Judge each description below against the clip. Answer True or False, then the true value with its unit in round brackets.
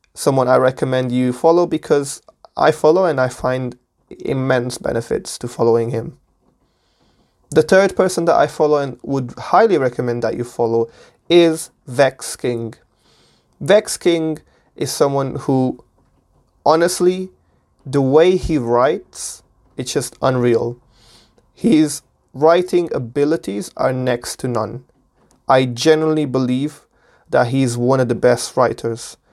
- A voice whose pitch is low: True (130 Hz)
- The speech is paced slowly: True (125 wpm)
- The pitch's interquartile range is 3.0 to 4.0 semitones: False (4.4 semitones)